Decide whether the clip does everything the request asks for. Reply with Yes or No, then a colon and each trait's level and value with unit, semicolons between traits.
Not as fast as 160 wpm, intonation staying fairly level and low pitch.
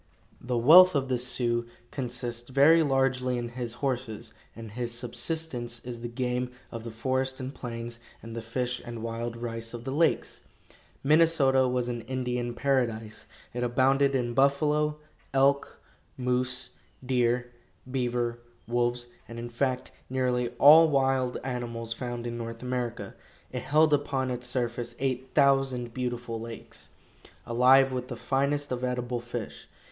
Yes: average, 145 wpm; narrow, 2.0 semitones; low, 125 Hz